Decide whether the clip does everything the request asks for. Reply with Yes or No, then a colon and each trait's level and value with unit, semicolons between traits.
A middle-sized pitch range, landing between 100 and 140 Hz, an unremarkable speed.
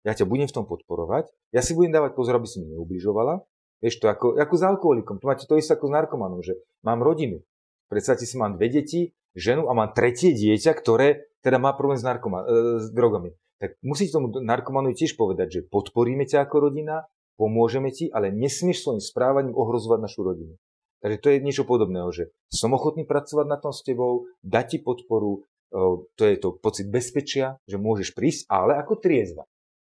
No: average, 4.9 semitones; low, 130 Hz; fast, 195 wpm